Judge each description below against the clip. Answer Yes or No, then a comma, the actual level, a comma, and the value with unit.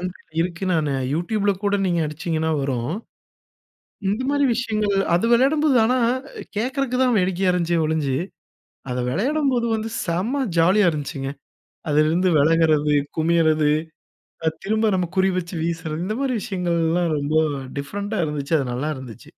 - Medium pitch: Yes, medium, 175 Hz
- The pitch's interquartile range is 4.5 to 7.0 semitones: Yes, wide, 5.5 semitones